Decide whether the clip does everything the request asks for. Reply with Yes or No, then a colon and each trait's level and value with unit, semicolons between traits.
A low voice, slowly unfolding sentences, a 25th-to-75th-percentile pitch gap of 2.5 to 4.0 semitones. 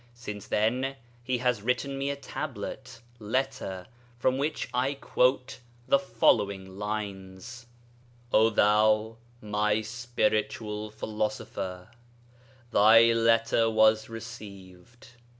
Yes: low, 110 Hz; slow, 95 wpm; average, 2.9 semitones